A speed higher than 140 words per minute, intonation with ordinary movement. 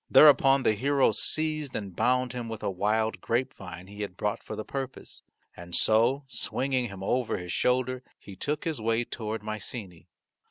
Yes: average, 170 wpm; average, 4.0 semitones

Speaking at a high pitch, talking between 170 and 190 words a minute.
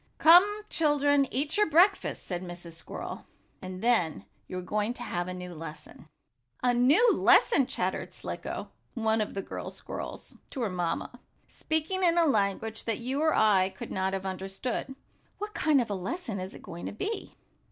Yes: high, 225 Hz; average, 180 wpm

